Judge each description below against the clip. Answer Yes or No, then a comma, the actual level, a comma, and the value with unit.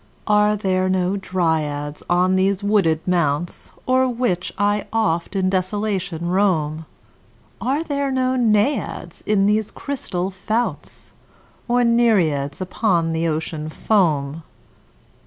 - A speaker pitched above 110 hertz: Yes, high, 190 Hz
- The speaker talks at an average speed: No, slow, 115 wpm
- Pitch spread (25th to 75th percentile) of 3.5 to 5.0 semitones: Yes, average, 4.5 semitones